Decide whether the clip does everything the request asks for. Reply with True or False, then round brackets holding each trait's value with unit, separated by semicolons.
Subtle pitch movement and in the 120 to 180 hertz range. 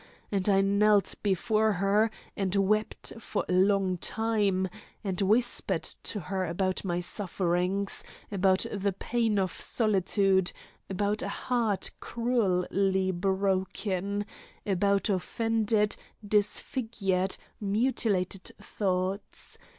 False (2.1 semitones; 195 Hz)